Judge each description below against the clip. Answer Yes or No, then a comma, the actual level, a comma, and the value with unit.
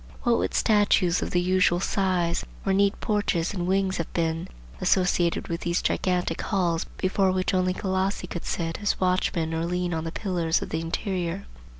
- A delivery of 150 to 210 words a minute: Yes, average, 180 wpm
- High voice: No, medium, 180 Hz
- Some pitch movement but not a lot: No, narrow, 2.2 semitones